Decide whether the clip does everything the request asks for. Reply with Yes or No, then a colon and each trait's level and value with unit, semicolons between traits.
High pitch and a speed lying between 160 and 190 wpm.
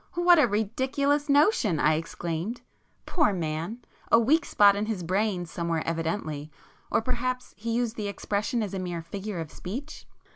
No: high, 205 Hz; average, 145 wpm